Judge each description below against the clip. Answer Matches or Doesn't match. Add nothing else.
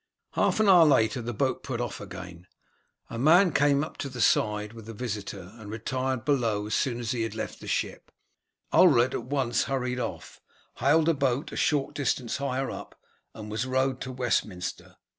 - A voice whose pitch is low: Matches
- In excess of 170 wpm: Matches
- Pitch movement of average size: Matches